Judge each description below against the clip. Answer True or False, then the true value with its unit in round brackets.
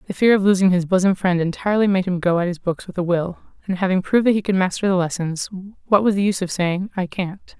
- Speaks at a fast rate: True (270 wpm)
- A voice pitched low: False (185 Hz)